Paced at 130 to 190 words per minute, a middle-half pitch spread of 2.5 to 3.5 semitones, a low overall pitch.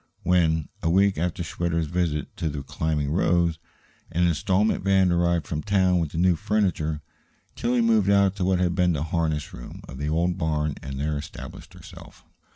Yes: average, 180 wpm; average, 3.0 semitones; very low, 85 Hz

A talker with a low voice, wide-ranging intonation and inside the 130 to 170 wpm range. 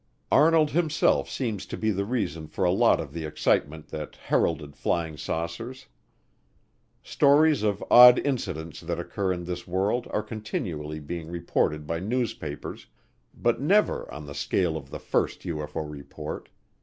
Yes: very low, 90 Hz; wide, 6.7 semitones; average, 150 wpm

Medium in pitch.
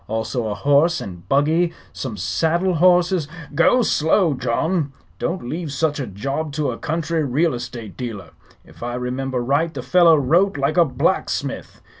Yes: medium, 145 Hz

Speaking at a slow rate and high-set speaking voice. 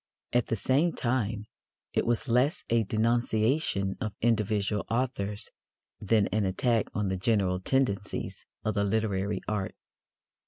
No: slow, 130 wpm; low, 110 Hz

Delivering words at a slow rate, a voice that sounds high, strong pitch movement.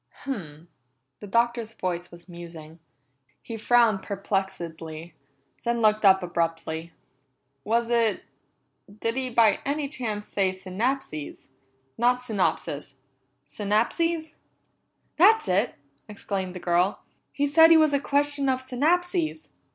Yes: slow, 115 wpm; high, 215 Hz; wide, 6.7 semitones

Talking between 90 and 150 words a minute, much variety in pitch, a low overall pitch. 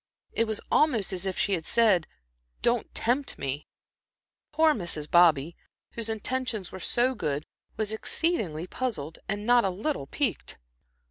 No: average, 145 wpm; wide, 5.9 semitones; high, 210 Hz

